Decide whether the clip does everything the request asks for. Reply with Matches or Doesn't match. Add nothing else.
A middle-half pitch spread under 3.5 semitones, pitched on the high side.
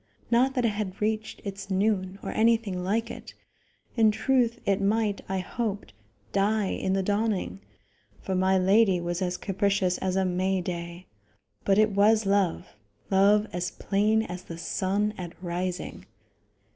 Matches